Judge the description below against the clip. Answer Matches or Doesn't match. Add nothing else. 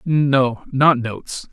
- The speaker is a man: Matches